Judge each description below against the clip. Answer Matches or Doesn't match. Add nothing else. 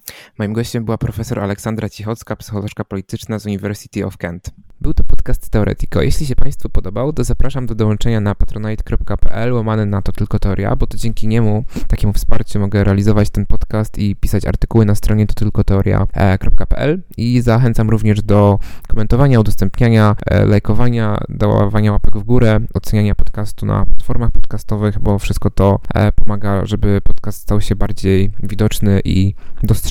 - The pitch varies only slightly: Matches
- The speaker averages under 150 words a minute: Doesn't match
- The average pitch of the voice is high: Doesn't match